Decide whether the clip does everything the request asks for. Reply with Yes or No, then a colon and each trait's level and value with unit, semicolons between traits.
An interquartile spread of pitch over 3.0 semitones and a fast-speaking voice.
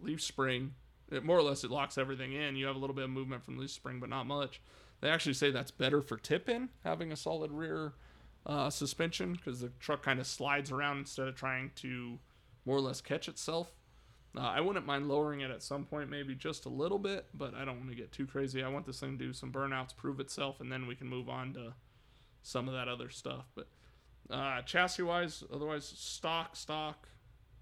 No: narrow, 2.4 semitones; fast, 225 wpm